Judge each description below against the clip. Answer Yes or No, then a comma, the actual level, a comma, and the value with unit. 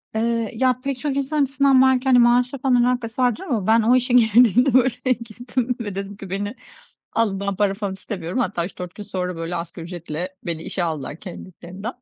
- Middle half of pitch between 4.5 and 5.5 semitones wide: Yes, average, 5.0 semitones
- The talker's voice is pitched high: Yes, high, 225 Hz